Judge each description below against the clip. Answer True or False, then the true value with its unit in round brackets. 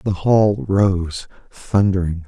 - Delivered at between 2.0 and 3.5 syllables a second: True (3.2 syllables/s)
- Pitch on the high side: False (95 Hz)